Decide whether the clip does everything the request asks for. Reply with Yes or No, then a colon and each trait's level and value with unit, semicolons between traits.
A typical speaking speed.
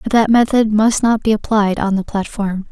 No: fast, 220 wpm